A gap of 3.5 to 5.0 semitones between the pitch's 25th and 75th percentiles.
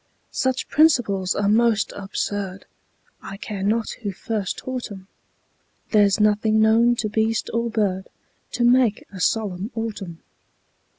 No: narrow, 2.6 semitones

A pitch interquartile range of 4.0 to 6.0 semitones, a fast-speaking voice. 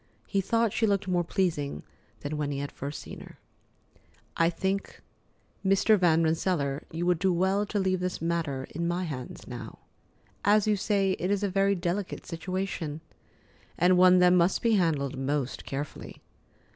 No: average, 4.3 semitones; average, 170 wpm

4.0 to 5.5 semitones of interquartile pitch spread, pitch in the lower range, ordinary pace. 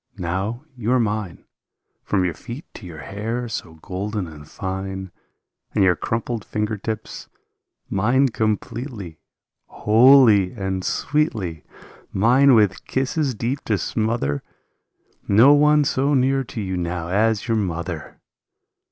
No: average, 4.7 semitones; low, 105 Hz; slow, 130 wpm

